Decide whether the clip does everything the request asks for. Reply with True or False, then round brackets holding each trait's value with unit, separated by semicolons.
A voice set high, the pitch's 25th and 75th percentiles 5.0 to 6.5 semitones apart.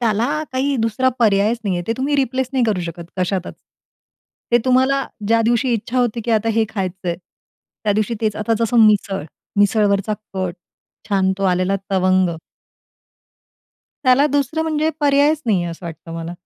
True (220 Hz; 5.3 semitones)